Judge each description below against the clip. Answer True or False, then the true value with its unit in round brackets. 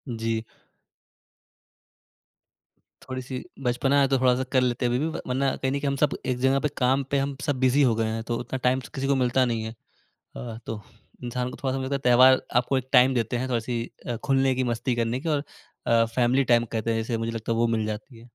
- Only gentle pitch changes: True (2.2 semitones)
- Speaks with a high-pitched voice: False (125 Hz)